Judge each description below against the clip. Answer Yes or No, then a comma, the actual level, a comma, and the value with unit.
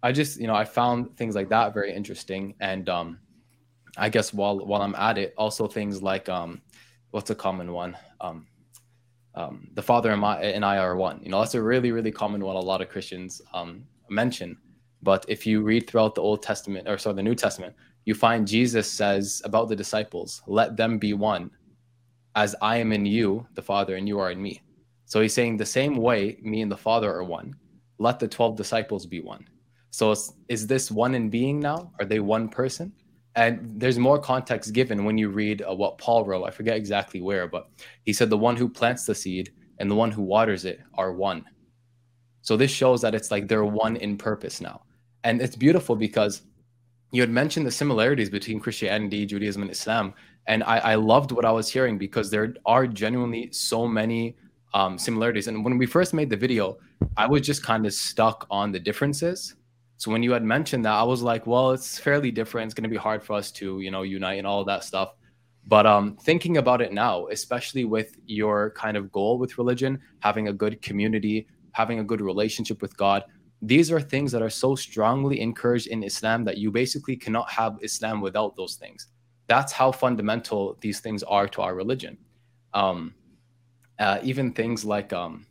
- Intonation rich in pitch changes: No, average, 2.7 semitones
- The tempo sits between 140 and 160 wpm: No, fast, 205 wpm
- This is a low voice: Yes, low, 110 Hz